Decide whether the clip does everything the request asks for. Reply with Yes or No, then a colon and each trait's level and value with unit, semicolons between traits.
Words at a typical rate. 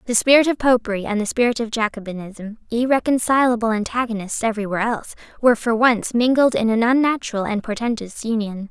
Yes: average, 165 wpm